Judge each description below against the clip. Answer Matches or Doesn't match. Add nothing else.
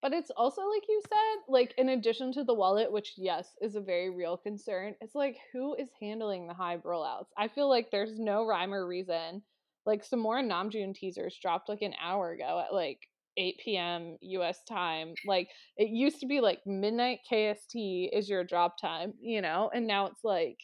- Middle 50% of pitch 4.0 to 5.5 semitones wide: Matches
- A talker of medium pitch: Doesn't match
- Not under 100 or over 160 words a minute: Doesn't match